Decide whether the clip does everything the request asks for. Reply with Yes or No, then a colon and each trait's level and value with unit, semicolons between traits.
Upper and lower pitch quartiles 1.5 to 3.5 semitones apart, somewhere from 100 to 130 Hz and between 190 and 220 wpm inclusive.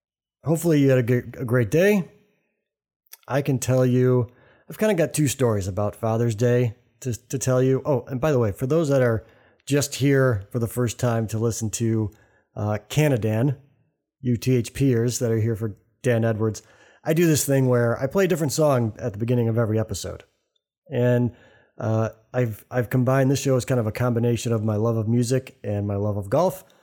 Yes: average, 3.0 semitones; low, 125 Hz; fast, 205 wpm